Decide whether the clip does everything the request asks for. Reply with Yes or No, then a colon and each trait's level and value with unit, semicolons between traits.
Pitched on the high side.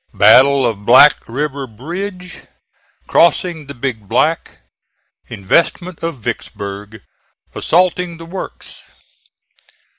No: medium, 140 Hz